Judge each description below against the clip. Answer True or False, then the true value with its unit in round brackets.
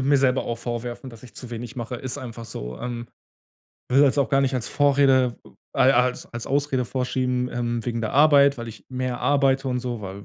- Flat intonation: True (2.3 semitones)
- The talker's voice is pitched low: True (125 Hz)